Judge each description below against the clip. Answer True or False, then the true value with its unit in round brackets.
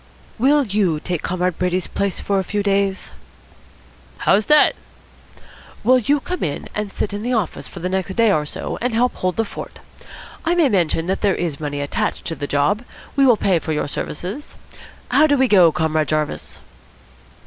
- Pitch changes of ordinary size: False (5.8 semitones)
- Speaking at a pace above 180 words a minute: True (190 wpm)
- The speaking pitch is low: False (195 Hz)